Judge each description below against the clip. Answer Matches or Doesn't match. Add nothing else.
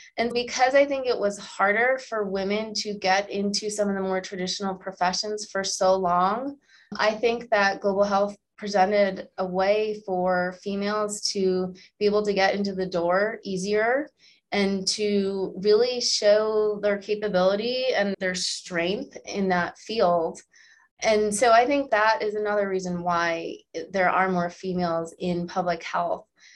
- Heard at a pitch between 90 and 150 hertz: Doesn't match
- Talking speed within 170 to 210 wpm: Doesn't match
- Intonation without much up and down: Matches